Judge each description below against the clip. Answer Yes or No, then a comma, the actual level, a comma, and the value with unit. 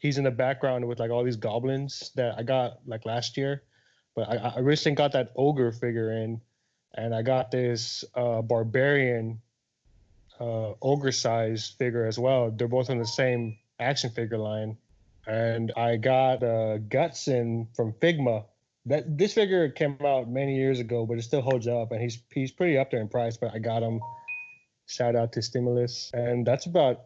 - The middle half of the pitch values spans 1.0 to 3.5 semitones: Yes, narrow, 2.5 semitones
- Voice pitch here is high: No, low, 120 Hz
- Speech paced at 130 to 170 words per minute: No, average, 185 wpm